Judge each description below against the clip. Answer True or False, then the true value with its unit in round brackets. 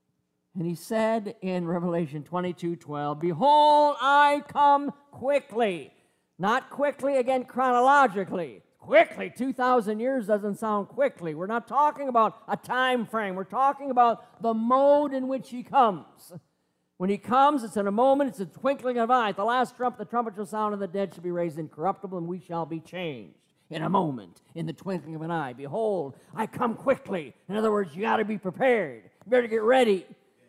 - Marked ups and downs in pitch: True (6.1 semitones)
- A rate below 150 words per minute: False (185 wpm)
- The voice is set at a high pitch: True (220 Hz)